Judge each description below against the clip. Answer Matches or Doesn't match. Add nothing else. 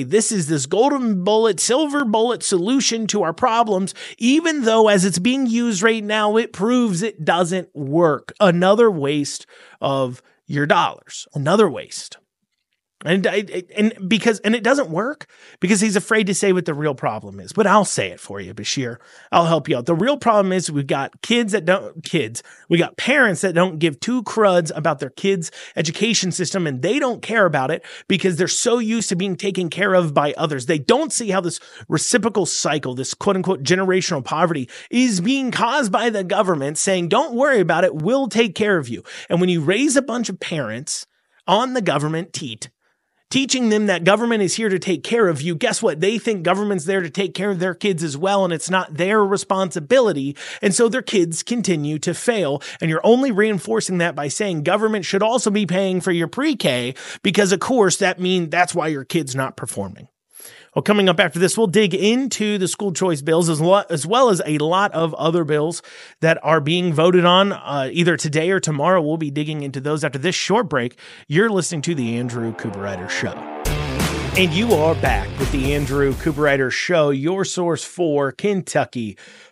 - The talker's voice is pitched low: Doesn't match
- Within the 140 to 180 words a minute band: Doesn't match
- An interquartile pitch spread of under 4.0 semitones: Doesn't match